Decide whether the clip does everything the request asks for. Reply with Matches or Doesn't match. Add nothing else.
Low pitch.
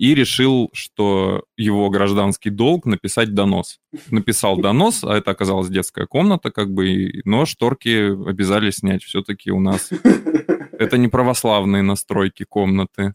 Matches